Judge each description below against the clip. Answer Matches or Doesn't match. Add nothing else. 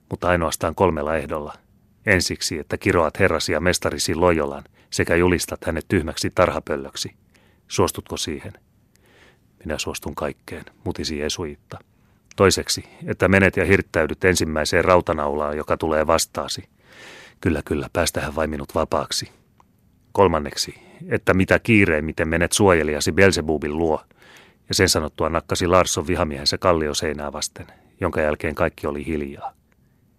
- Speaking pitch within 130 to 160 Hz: Doesn't match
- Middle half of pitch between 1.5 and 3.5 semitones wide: Doesn't match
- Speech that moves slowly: Doesn't match